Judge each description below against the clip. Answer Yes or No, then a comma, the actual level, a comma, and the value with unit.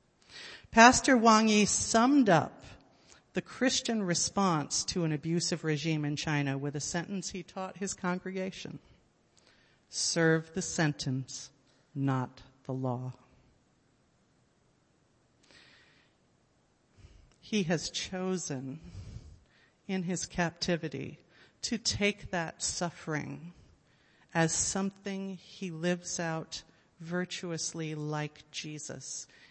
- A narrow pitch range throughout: No, average, 4.2 semitones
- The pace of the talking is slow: Yes, slow, 90 wpm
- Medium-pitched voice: Yes, medium, 165 Hz